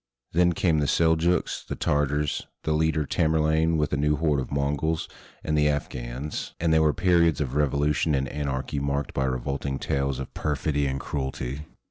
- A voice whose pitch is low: Yes, very low, 75 Hz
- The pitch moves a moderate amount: No, narrow, 2.3 semitones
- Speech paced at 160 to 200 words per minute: Yes, average, 170 wpm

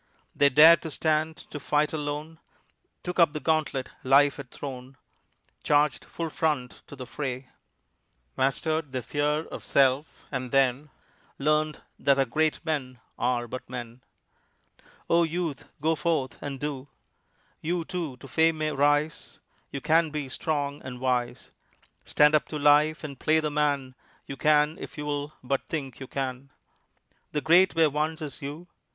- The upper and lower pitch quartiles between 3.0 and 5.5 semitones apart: No, narrow, 2.6 semitones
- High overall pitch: No, medium, 145 Hz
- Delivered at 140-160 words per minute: Yes, average, 155 wpm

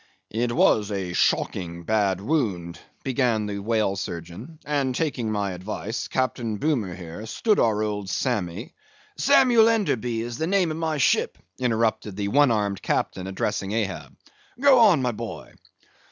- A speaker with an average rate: Yes, average, 145 wpm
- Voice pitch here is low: Yes, low, 110 Hz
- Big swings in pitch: Yes, wide, 5.7 semitones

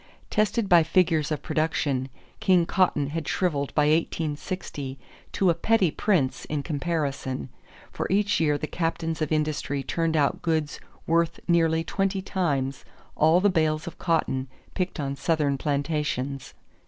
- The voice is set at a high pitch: No, medium, 160 Hz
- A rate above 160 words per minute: No, average, 140 wpm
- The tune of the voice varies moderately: Yes, average, 3.2 semitones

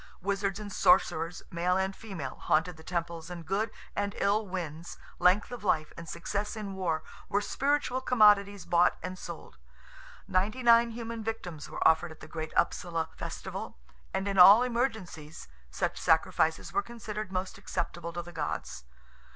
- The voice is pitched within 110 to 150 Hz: No, high, 190 Hz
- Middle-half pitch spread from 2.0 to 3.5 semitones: No, average, 3.9 semitones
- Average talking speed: Yes, average, 160 wpm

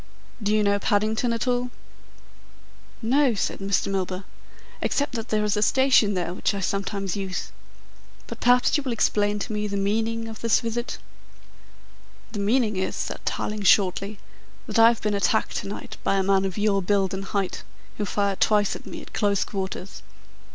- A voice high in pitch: Yes, high, 205 Hz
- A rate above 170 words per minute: Yes, average, 180 wpm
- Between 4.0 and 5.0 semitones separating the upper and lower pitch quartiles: No, narrow, 2.4 semitones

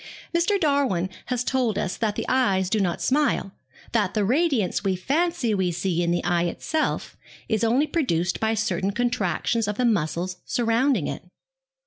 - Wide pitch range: Yes, wide, 5.7 semitones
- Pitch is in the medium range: No, high, 220 Hz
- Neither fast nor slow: Yes, average, 165 wpm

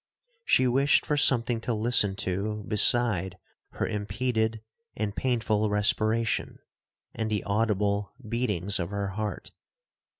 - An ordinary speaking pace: No, slow, 120 wpm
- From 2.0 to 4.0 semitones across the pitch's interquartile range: Yes, narrow, 2.4 semitones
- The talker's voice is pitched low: Yes, low, 110 Hz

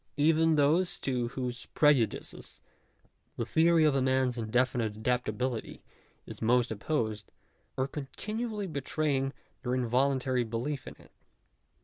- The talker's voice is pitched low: Yes, low, 130 Hz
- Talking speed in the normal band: No, slow, 115 wpm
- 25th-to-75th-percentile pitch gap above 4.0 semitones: No, average, 3.6 semitones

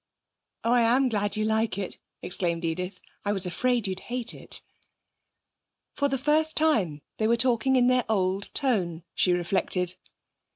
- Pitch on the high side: Yes, high, 215 Hz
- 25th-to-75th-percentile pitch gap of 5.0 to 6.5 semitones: Yes, average, 5.3 semitones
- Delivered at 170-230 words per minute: No, average, 160 wpm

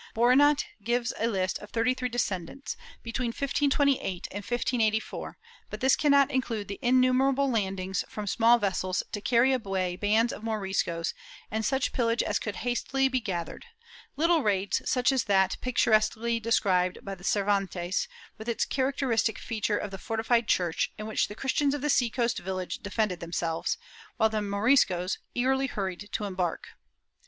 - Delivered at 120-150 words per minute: No, average, 160 wpm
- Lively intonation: No, average, 4.4 semitones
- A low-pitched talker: No, high, 220 Hz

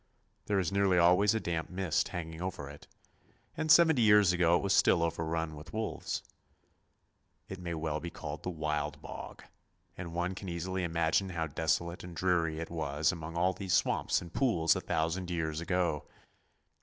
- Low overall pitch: Yes, very low, 85 Hz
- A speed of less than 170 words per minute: No, average, 175 wpm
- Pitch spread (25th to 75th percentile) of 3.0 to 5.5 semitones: No, narrow, 2.5 semitones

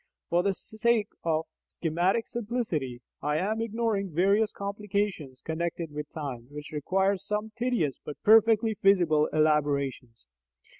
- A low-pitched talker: No, medium, 185 Hz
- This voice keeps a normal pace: No, slow, 120 wpm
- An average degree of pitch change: No, wide, 5.9 semitones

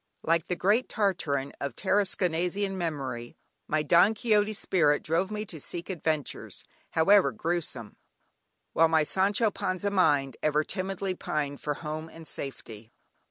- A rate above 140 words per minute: No, slow, 135 wpm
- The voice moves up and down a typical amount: Yes, average, 4.4 semitones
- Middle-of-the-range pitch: Yes, medium, 170 Hz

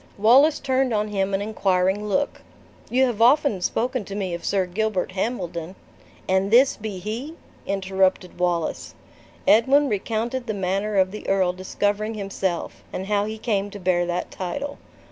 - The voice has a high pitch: Yes, high, 205 Hz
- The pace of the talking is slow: No, average, 165 wpm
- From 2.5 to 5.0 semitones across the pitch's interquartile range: Yes, average, 3.4 semitones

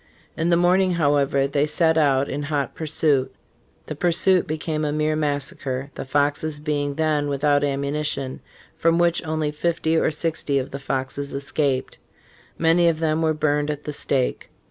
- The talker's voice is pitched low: No, medium, 150 Hz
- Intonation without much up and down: Yes, narrow, 2.1 semitones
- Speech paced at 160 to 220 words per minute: Yes, average, 165 wpm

